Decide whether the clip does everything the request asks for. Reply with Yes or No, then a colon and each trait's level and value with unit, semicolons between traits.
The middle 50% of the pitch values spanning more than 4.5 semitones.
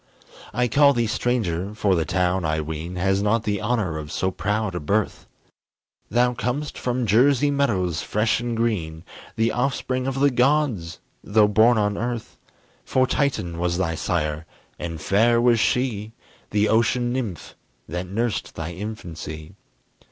Yes: wide, 5.6 semitones